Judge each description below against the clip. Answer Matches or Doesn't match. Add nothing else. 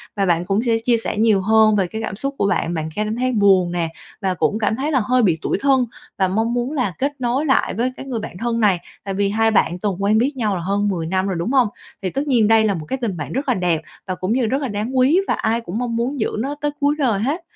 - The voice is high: Matches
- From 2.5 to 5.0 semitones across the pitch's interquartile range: Matches